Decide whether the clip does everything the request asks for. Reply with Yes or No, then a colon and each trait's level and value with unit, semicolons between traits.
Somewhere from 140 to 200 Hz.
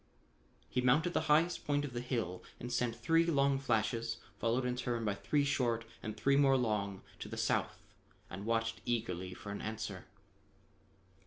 No: low, 120 Hz